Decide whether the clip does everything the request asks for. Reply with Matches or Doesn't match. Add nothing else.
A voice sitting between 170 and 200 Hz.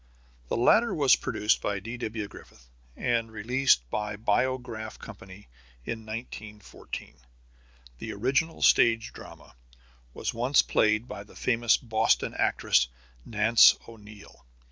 Doesn't match